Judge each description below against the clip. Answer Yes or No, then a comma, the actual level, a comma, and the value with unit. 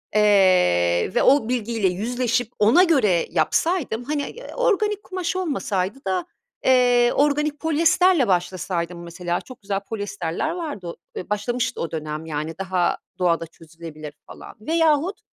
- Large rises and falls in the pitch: Yes, wide, 8.9 semitones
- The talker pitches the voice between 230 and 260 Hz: No, high, 215 Hz